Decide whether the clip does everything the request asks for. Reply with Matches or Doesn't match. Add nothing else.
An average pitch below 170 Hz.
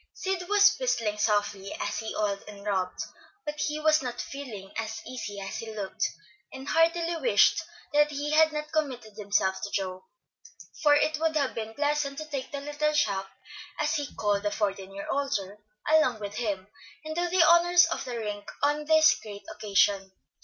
Doesn't match